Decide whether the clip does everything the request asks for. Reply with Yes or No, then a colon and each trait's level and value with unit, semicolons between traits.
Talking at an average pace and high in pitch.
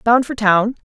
Yes: average, 195 wpm; high, 225 Hz